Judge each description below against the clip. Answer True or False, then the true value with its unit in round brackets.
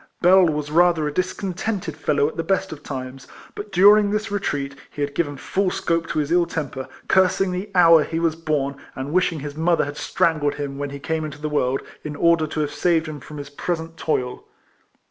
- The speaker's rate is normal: False (210 wpm)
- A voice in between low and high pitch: True (160 Hz)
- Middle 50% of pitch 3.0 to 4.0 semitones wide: True (3.6 semitones)